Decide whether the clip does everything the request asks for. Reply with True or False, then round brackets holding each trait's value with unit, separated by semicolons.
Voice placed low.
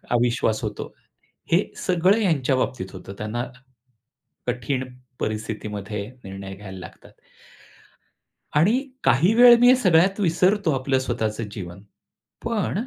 True (130 Hz)